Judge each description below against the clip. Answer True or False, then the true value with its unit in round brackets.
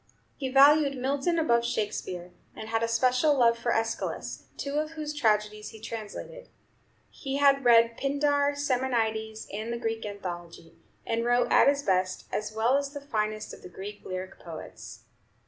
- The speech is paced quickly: False (165 wpm)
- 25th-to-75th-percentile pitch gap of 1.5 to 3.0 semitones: False (4.6 semitones)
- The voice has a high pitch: True (235 Hz)